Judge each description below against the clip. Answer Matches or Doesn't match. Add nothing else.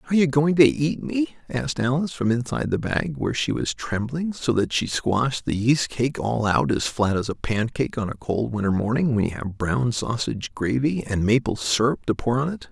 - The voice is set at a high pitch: Doesn't match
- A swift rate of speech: Matches